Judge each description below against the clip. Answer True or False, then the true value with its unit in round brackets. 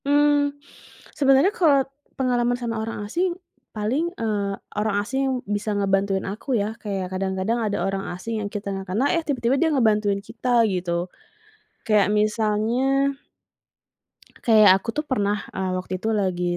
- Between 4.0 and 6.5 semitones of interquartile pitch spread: True (5.0 semitones)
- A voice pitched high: True (220 Hz)